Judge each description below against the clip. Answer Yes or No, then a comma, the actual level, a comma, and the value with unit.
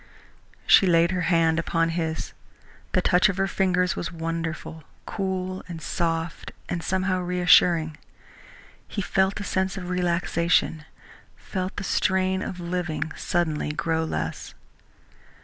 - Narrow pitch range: Yes, narrow, 2.2 semitones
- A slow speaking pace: Yes, slow, 130 wpm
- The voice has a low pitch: No, medium, 175 Hz